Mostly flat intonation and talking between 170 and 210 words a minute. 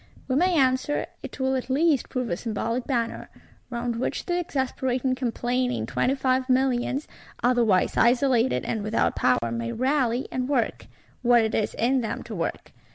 No: narrow, 2.2 semitones; average, 160 wpm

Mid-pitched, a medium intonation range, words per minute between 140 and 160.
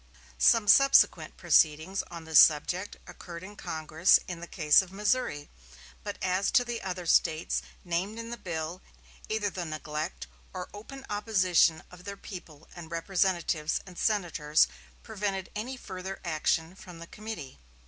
Yes: medium, 180 Hz; average, 4.1 semitones; average, 150 wpm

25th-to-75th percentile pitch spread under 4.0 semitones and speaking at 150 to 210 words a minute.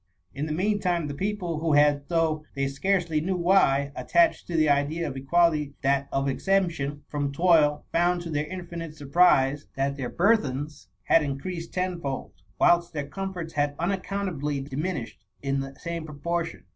Yes: average, 3.6 semitones; average, 160 wpm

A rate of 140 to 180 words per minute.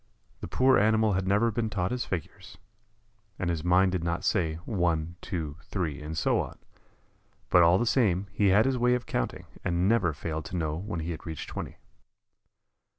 No: average, 190 wpm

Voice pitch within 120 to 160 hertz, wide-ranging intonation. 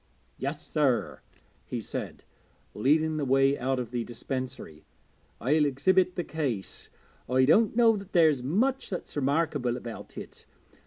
No: medium, 140 Hz; average, 4.6 semitones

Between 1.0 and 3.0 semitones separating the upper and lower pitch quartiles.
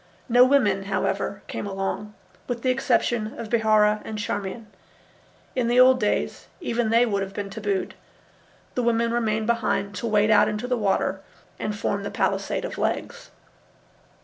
Yes: average, 2.7 semitones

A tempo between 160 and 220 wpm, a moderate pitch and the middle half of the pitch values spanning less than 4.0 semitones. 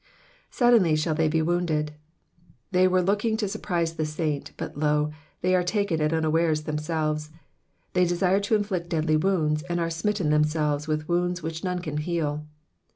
Yes: average, 165 wpm; medium, 165 Hz; average, 2.9 semitones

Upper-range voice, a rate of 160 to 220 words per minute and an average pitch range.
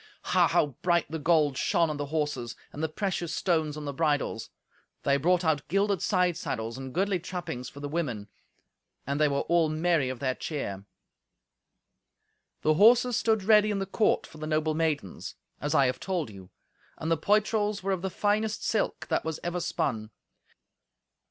No: medium, 160 Hz; average, 180 wpm; average, 4.6 semitones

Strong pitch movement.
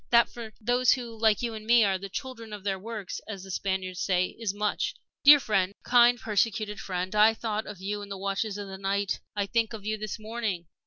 No: average, 2.7 semitones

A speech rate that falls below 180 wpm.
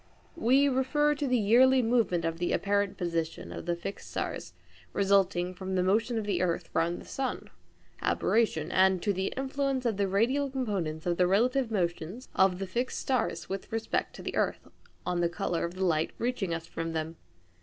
No: average, 190 wpm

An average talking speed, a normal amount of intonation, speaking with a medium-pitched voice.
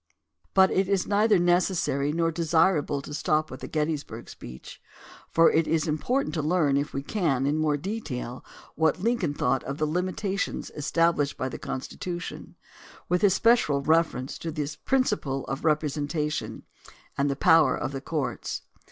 Yes: average, 160 wpm; average, 4.0 semitones; medium, 155 Hz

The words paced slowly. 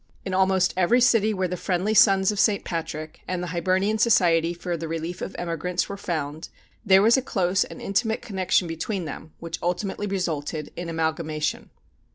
No: average, 180 wpm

